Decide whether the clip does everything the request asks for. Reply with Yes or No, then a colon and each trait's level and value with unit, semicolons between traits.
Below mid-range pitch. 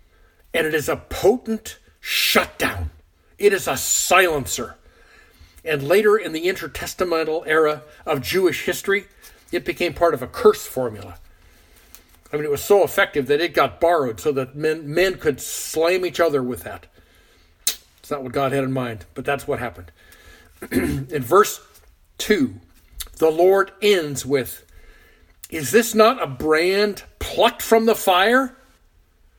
No: medium, 150 Hz